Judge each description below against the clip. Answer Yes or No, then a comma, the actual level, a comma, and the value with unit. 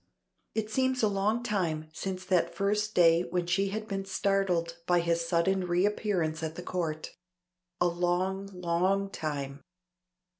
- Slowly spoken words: No, average, 145 wpm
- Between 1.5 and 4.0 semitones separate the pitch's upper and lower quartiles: Yes, average, 2.7 semitones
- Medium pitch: Yes, medium, 180 Hz